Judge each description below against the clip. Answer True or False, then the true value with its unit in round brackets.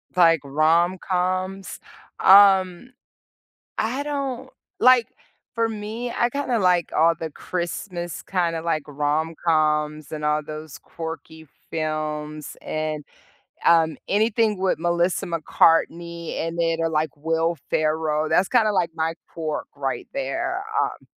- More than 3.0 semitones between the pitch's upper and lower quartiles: True (3.8 semitones)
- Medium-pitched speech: True (170 Hz)